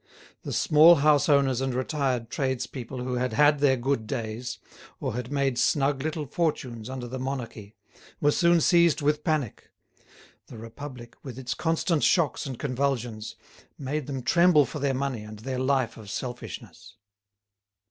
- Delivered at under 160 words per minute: Yes, average, 150 wpm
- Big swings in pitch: No, average, 3.2 semitones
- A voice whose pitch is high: No, low, 135 Hz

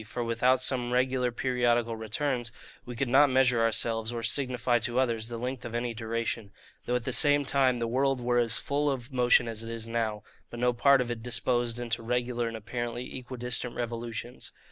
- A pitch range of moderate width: No, narrow, 1.5 semitones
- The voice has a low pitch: Yes, low, 120 Hz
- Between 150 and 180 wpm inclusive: No, average, 195 wpm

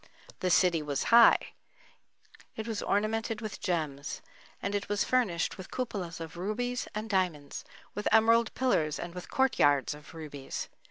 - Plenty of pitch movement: Yes, wide, 5.7 semitones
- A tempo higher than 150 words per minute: No, average, 145 wpm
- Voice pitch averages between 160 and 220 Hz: Yes, high, 190 Hz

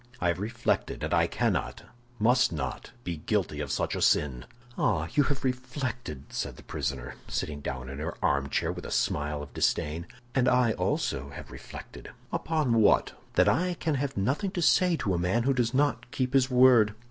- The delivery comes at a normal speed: Yes, average, 190 wpm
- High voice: No, low, 115 Hz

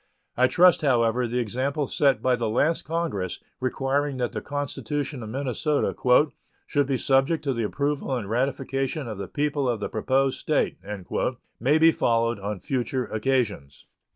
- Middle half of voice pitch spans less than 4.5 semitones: Yes, average, 3.5 semitones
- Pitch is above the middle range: No, low, 130 Hz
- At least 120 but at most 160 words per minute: Yes, average, 155 wpm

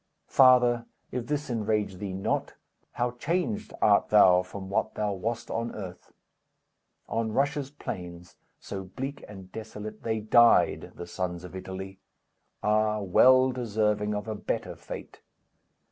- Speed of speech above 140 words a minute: No, slow, 135 wpm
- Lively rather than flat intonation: No, average, 4.0 semitones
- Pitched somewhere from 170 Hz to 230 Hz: No, low, 105 Hz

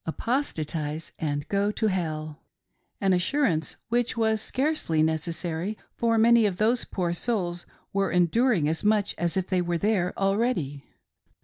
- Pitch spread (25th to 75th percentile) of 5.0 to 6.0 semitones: Yes, average, 5.3 semitones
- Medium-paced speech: Yes, average, 155 wpm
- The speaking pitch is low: No, medium, 185 Hz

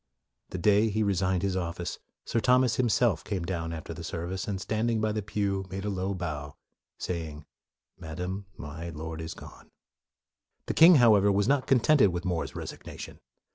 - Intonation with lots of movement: No, average, 4.2 semitones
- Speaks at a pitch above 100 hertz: No, very low, 95 Hz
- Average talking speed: Yes, average, 175 wpm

